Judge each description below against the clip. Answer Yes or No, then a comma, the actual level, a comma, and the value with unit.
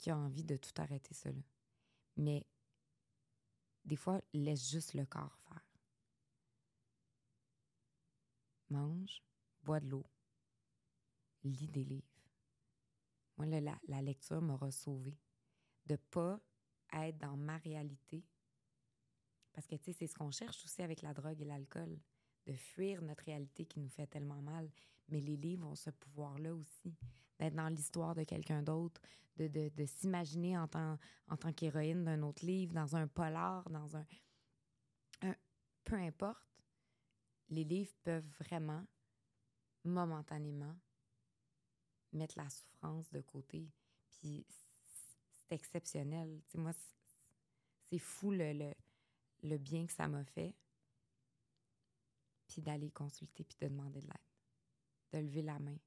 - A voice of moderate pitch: Yes, medium, 150 Hz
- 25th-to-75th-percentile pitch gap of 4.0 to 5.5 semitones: No, average, 3.2 semitones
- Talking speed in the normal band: No, slow, 140 wpm